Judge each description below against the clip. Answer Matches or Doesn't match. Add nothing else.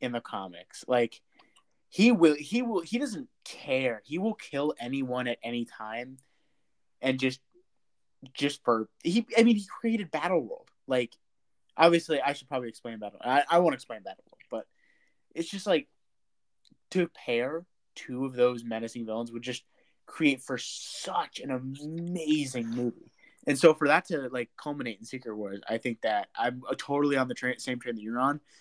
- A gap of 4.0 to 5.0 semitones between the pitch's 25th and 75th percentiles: Doesn't match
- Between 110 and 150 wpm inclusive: Doesn't match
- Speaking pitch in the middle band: Doesn't match